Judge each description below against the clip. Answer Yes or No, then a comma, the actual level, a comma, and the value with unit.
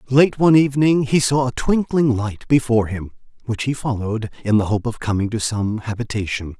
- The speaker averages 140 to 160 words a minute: No, average, 190 wpm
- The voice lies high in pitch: No, low, 120 Hz